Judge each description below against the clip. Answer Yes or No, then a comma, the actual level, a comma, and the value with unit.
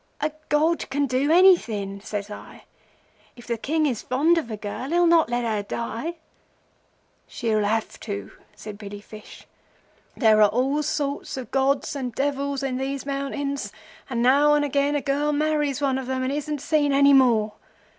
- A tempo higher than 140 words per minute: Yes, average, 175 wpm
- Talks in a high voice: Yes, very high, 275 Hz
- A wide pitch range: No, average, 4.1 semitones